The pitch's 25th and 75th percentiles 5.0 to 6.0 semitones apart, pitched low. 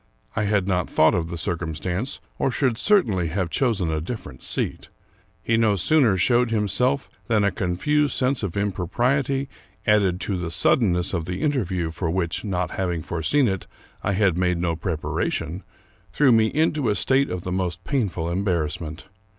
Yes: wide, 5.5 semitones; very low, 95 Hz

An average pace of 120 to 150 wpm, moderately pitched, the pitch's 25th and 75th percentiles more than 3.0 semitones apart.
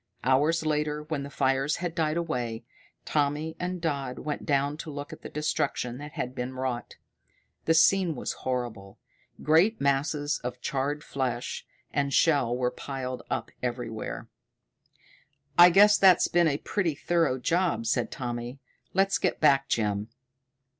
Yes: average, 145 wpm; medium, 145 Hz; average, 4.2 semitones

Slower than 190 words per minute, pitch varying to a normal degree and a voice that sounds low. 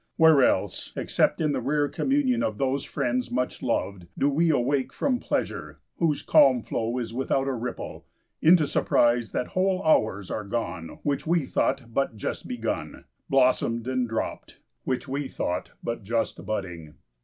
Yes: average, 160 wpm; average, 4.1 semitones; low, 130 Hz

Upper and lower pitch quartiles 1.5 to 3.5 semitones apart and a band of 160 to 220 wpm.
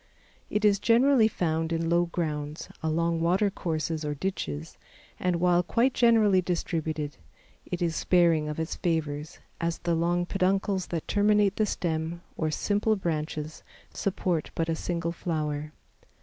No: average, 3.2 semitones; average, 145 wpm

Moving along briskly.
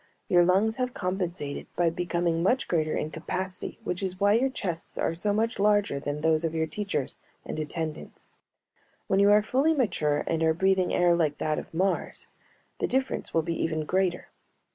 No: average, 185 wpm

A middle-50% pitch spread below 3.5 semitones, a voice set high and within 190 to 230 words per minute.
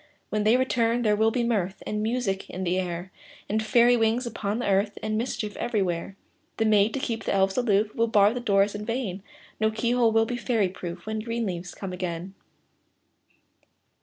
Yes: average, 3.1 semitones; high, 215 Hz; average, 195 wpm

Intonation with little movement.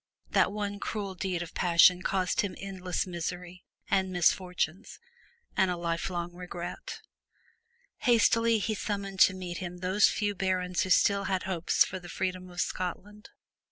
Yes: narrow, 1.9 semitones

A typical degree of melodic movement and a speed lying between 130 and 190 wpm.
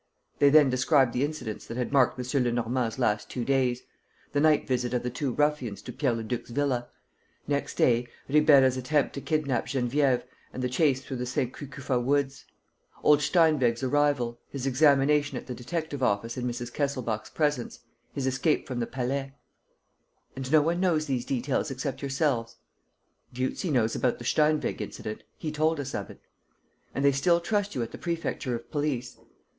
Yes: average, 3.1 semitones; average, 175 wpm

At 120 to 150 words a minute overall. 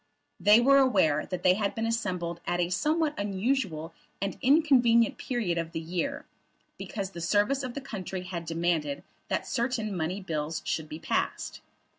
No: average, 165 wpm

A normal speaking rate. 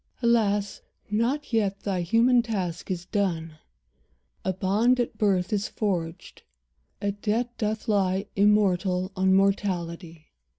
No: slow, 120 wpm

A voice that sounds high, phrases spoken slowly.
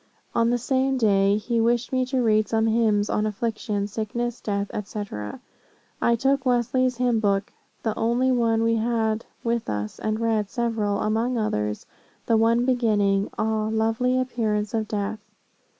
No: high, 225 Hz; average, 155 wpm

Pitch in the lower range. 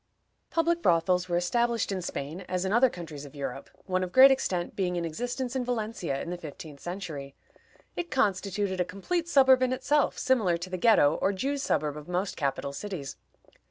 No: medium, 185 Hz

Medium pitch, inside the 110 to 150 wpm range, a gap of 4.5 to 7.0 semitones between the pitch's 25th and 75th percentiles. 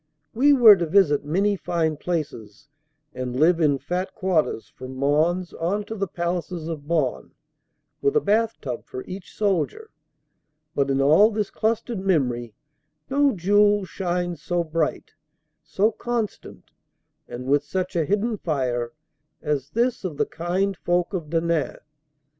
Yes: medium, 175 Hz; average, 145 wpm; wide, 5.5 semitones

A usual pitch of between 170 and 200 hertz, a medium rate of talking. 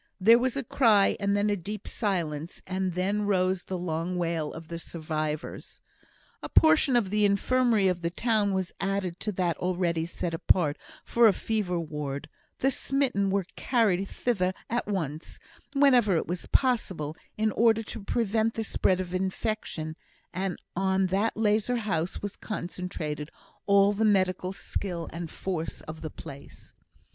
Yes: high, 190 Hz; average, 160 wpm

